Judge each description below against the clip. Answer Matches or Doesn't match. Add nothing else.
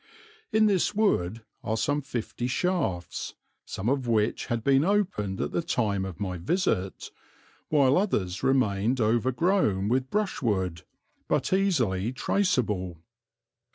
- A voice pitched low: Matches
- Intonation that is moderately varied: Doesn't match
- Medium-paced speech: Doesn't match